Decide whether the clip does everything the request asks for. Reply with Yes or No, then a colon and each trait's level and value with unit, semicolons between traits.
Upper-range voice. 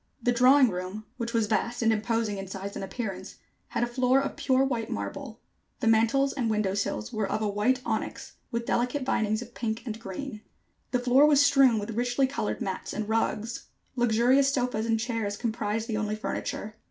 Yes: high, 225 Hz